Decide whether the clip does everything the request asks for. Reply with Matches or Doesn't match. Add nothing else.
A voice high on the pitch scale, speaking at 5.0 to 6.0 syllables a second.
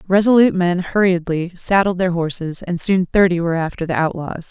Doesn't match